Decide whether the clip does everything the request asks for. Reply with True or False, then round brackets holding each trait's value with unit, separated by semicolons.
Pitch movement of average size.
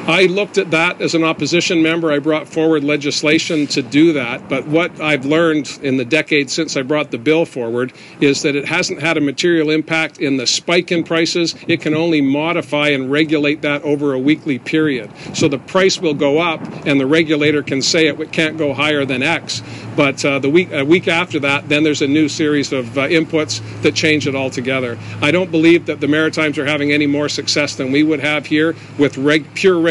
False (2.2 semitones)